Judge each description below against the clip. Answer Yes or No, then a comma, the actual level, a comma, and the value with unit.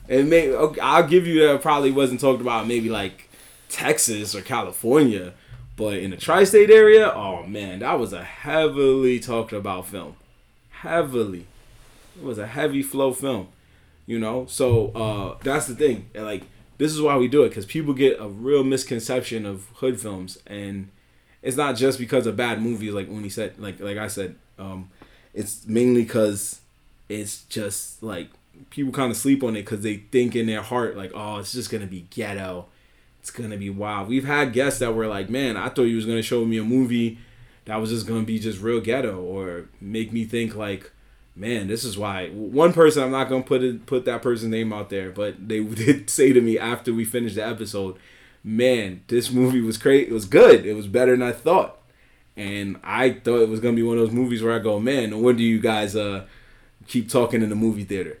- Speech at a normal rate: No, fast, 210 wpm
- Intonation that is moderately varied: Yes, average, 3.4 semitones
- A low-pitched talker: Yes, low, 115 Hz